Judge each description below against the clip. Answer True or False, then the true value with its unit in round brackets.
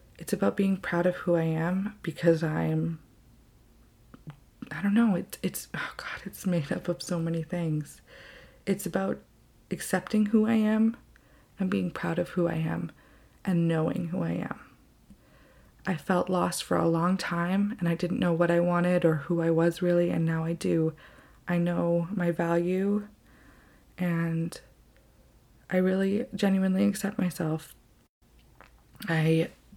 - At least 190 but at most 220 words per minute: False (155 wpm)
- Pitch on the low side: False (175 Hz)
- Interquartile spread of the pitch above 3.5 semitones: False (2.4 semitones)